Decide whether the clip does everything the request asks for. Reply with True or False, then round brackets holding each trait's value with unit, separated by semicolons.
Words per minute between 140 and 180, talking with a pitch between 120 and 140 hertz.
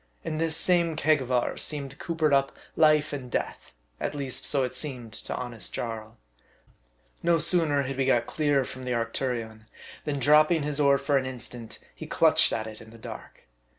False (190 wpm; 135 Hz)